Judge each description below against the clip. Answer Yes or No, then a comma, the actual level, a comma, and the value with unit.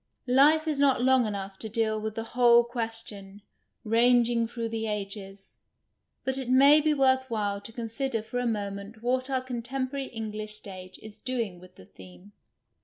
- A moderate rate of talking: Yes, average, 180 wpm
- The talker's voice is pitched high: Yes, high, 230 Hz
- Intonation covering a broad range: No, average, 3.6 semitones